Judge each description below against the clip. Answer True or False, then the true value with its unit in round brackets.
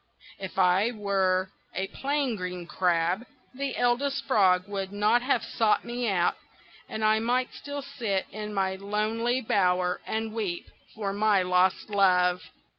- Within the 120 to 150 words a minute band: True (145 wpm)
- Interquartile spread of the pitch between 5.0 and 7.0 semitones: False (4.1 semitones)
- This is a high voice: True (205 Hz)